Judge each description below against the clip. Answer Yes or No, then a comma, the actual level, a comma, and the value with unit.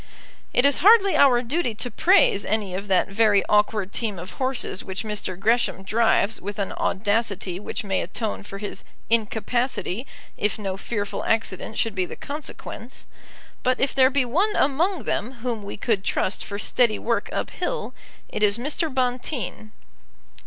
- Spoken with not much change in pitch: No, average, 4.1 semitones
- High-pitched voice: Yes, high, 225 Hz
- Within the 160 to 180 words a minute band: Yes, average, 165 wpm